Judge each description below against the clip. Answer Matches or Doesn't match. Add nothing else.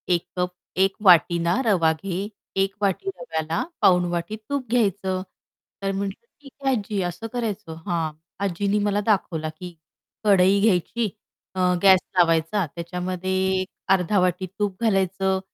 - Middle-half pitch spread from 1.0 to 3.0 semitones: Matches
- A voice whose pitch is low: Doesn't match